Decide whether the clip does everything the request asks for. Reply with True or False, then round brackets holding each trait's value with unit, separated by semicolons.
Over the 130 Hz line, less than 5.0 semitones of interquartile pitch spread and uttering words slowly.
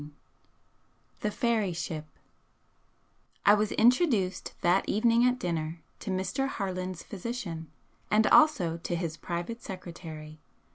False (185 Hz; 5.3 semitones; 115 wpm)